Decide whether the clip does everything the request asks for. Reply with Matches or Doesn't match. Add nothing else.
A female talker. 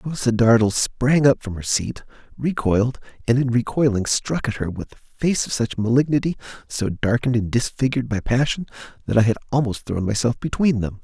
Doesn't match